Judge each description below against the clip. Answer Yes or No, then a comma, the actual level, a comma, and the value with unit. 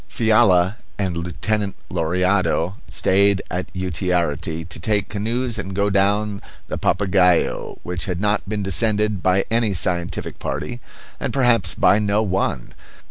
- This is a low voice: Yes, very low, 95 Hz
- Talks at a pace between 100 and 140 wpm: Yes, slow, 135 wpm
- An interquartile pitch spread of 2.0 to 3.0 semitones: Yes, average, 2.7 semitones